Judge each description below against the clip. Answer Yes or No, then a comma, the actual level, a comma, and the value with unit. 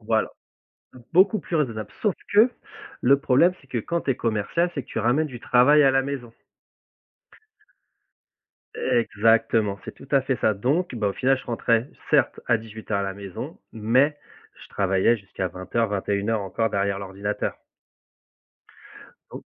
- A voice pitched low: Yes, low, 115 Hz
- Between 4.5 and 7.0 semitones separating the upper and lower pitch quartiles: Yes, average, 4.9 semitones